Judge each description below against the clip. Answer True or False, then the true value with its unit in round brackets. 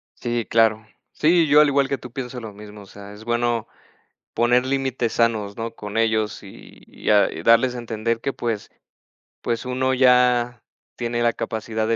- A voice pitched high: False (115 Hz)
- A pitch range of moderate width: False (2.2 semitones)